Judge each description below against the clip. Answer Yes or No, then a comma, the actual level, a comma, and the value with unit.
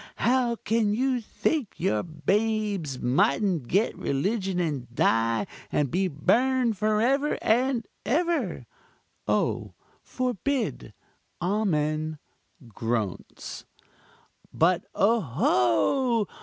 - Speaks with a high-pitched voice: Yes, high, 200 Hz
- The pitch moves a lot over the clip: Yes, wide, 8.0 semitones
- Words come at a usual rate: No, slow, 90 wpm